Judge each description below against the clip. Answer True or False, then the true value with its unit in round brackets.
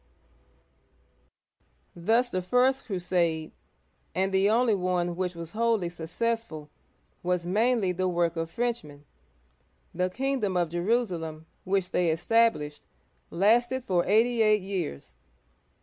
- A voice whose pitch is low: False (185 Hz)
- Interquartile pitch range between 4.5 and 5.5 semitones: True (4.9 semitones)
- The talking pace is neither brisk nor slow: False (120 wpm)